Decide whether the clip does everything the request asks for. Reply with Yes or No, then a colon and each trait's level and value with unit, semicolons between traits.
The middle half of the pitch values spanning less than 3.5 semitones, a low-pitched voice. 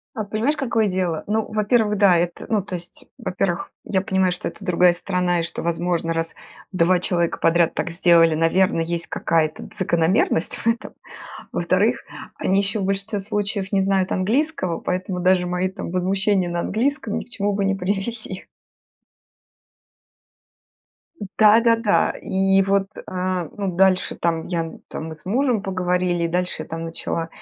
No: average, 2.7 semitones; medium, 185 Hz